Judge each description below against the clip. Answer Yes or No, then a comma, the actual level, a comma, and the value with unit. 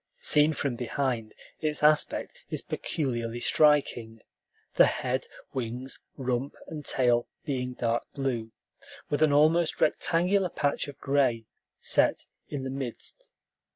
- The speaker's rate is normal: No, slow, 120 wpm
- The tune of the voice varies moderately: Yes, average, 3.7 semitones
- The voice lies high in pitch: No, low, 135 Hz